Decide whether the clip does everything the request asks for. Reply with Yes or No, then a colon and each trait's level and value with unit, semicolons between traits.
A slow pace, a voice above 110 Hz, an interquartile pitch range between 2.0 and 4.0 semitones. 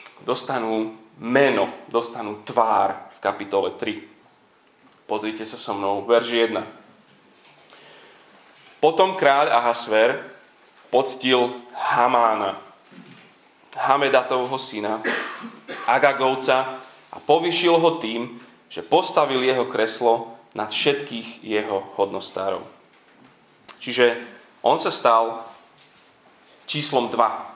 Yes: slow, 85 wpm; low, 120 Hz; average, 2.8 semitones